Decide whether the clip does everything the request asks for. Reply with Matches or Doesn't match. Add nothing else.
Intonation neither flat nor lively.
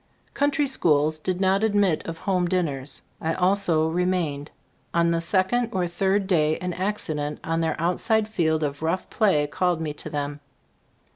Matches